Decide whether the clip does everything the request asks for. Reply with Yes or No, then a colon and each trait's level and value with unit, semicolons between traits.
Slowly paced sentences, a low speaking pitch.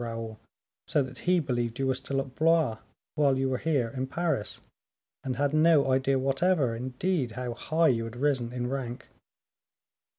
No: average, 170 wpm; low, 130 Hz